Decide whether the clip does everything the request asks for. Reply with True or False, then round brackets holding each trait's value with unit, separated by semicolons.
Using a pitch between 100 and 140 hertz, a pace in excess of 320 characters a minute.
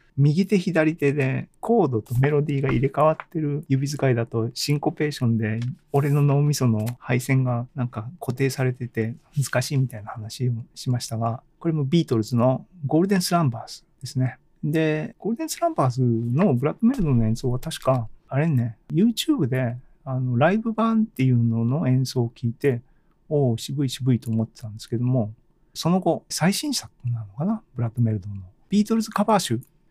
True (135 Hz; 380 characters per minute)